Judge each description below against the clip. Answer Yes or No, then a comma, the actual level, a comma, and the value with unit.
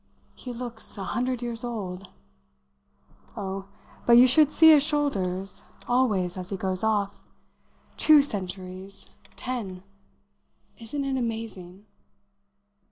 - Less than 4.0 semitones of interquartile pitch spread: No, average, 5.0 semitones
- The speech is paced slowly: Yes, slow, 110 wpm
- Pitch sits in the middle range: No, high, 220 Hz